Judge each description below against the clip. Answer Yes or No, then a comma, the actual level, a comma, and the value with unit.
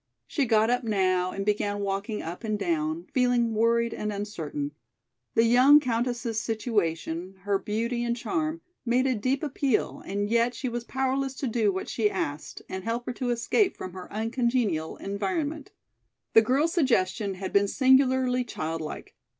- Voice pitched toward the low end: No, high, 225 Hz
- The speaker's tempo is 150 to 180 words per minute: Yes, average, 160 wpm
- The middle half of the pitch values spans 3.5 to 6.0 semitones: Yes, average, 4.2 semitones